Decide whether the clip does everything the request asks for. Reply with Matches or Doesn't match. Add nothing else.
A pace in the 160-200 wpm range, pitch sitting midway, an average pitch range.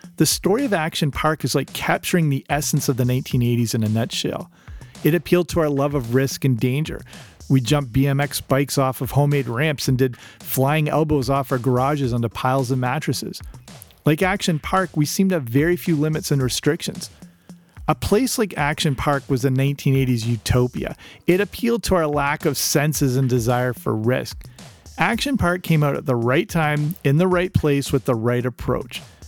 Matches